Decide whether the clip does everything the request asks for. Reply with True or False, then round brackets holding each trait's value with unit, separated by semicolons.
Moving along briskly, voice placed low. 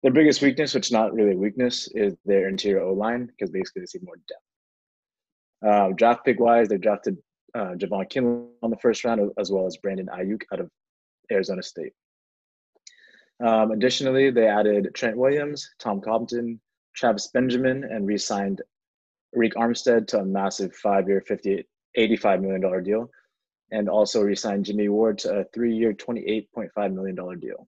False (160 wpm; 110 Hz)